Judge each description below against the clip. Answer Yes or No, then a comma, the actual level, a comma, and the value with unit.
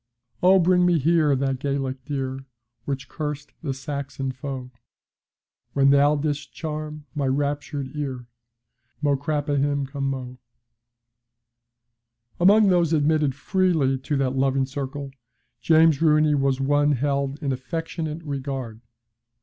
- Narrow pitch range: Yes, narrow, 2.2 semitones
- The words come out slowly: Yes, slow, 115 wpm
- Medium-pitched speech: Yes, medium, 145 Hz